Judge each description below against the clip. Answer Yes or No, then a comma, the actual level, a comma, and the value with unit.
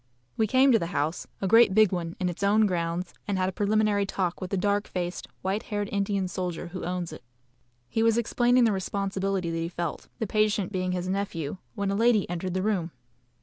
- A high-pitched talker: Yes, high, 195 Hz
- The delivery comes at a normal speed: No, fast, 215 wpm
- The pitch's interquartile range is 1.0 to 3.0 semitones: Yes, average, 2.7 semitones